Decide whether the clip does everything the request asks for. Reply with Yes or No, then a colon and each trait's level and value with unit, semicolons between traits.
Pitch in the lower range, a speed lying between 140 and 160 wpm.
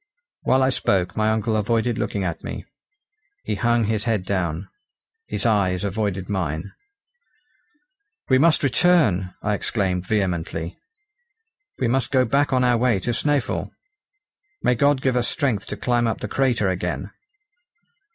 Yes: low, 110 Hz; average, 145 wpm